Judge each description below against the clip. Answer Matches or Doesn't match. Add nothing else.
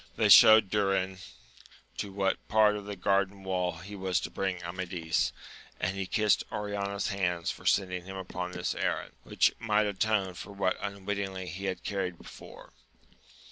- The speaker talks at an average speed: Matches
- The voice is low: Matches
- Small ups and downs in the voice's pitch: Matches